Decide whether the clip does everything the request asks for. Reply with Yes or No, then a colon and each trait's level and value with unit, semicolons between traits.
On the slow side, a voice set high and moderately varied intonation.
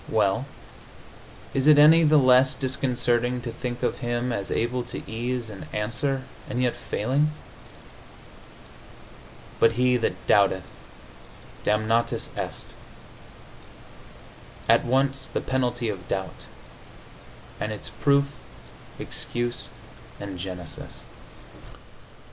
No: slow, 100 wpm; low, 120 Hz; average, 3.2 semitones